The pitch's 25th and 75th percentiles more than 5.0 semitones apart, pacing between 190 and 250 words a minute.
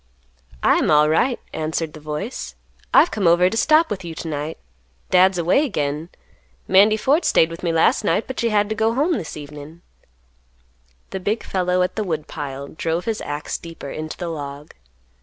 No: wide, 5.4 semitones; average, 180 wpm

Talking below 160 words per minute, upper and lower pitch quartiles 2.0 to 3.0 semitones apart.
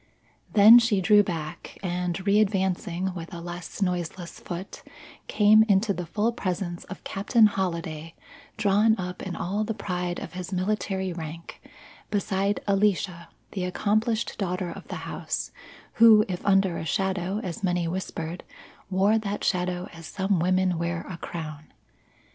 Yes: average, 145 wpm; average, 2.7 semitones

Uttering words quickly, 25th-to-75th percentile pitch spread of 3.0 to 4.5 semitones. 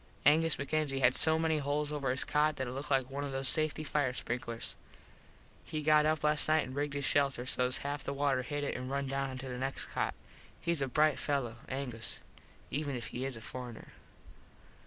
No: fast, 210 wpm; narrow, 2.6 semitones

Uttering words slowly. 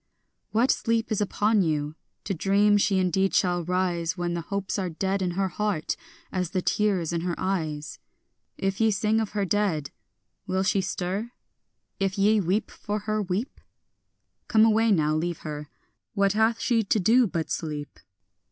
No: average, 170 wpm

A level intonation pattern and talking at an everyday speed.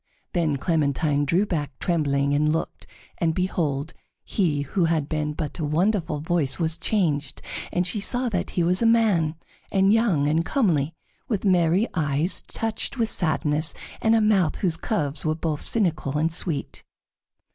No: average, 4.2 semitones; average, 160 wpm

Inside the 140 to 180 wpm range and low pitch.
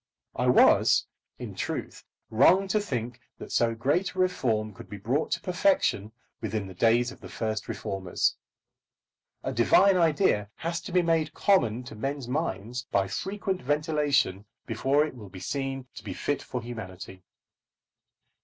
Yes: average, 155 wpm; low, 125 Hz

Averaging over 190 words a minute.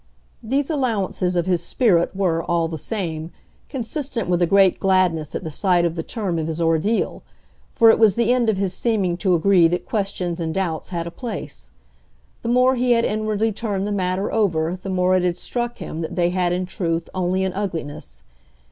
Yes: average, 200 wpm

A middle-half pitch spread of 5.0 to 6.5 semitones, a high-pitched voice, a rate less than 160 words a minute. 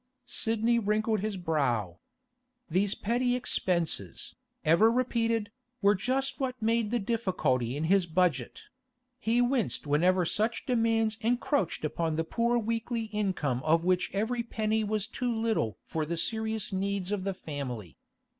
Yes: wide, 5.6 semitones; high, 210 Hz; average, 140 wpm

